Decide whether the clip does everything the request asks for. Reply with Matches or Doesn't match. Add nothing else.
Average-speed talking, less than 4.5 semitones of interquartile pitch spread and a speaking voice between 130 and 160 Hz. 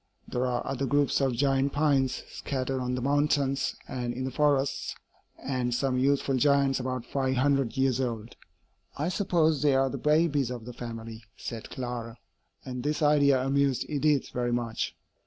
Matches